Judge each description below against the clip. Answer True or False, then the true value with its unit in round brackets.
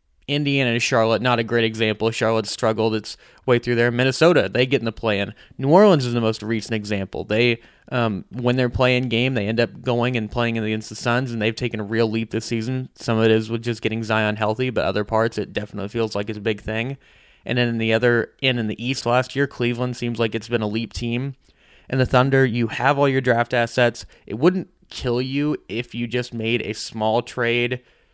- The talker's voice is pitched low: True (120 Hz)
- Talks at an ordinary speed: False (230 wpm)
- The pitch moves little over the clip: True (2.1 semitones)